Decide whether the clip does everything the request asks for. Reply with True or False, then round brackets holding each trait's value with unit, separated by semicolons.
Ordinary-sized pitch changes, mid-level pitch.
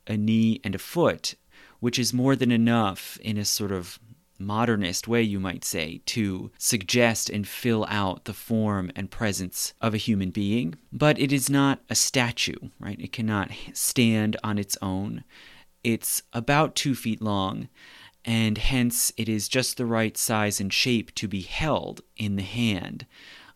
False (3.0 semitones; 110 Hz)